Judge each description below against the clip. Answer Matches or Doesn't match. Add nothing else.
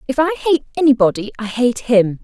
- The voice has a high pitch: Matches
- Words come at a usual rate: Matches